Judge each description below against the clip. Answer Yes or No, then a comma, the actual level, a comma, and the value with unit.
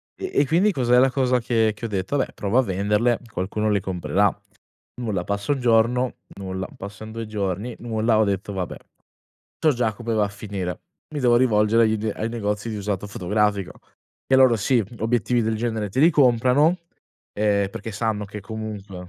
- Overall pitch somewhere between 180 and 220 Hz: No, low, 110 Hz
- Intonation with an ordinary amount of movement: Yes, average, 3.0 semitones